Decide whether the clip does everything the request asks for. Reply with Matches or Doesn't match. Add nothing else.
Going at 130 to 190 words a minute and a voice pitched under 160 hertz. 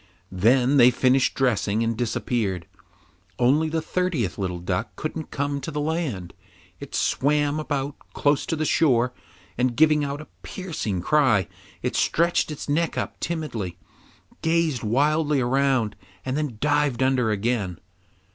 Matches